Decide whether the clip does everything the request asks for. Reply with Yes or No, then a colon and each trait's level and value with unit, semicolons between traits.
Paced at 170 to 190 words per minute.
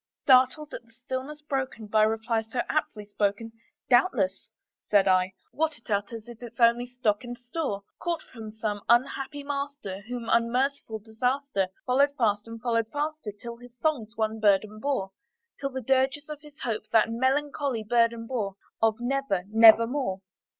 No: average, 155 wpm